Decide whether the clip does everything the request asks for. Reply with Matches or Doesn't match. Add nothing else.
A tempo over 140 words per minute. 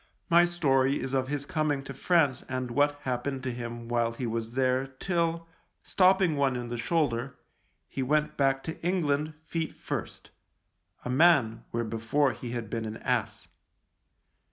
Matches